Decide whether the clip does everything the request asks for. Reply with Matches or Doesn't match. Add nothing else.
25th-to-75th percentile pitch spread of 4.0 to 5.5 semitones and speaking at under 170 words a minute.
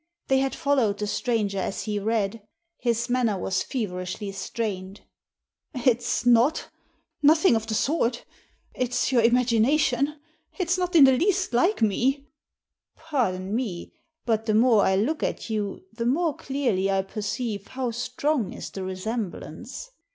Matches